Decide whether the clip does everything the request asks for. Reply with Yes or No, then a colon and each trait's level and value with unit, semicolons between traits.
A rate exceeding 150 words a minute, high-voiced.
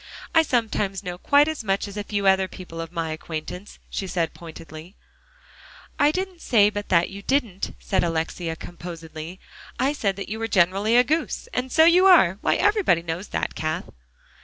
Yes: average, 180 wpm; high, 195 Hz